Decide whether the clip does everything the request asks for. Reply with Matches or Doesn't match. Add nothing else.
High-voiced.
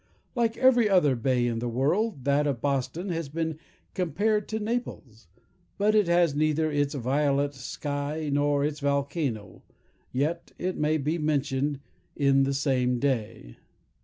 Doesn't match